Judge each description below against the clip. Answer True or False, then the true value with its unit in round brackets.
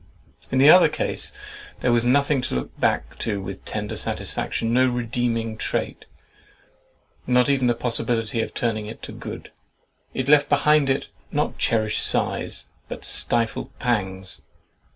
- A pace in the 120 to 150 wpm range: True (145 wpm)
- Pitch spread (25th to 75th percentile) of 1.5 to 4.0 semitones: True (3.0 semitones)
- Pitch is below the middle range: True (120 Hz)